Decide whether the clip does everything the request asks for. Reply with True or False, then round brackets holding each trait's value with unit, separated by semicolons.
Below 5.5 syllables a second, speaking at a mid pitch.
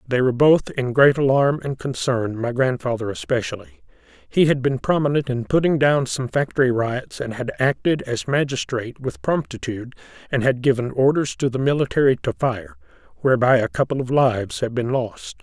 False (5.3 syllables/s; 130 Hz)